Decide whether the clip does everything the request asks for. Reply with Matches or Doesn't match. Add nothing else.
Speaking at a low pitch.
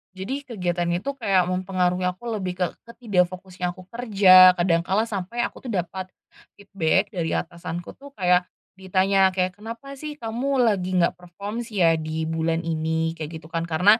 Doesn't match